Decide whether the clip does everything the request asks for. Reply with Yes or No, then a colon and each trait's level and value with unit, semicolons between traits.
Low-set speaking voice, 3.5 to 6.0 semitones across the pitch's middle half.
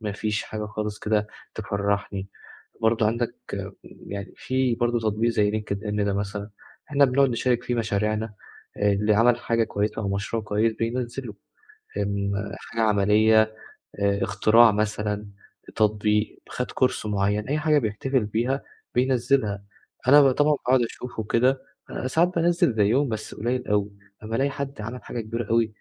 No: low, 110 Hz; average, 3.0 semitones